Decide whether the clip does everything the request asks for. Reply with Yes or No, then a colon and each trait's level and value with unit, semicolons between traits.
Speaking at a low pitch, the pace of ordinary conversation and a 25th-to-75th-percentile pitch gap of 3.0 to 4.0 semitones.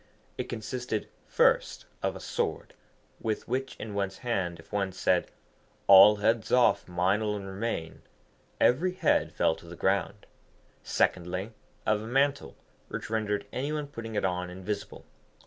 Yes: low, 105 Hz; average, 145 wpm; average, 3.6 semitones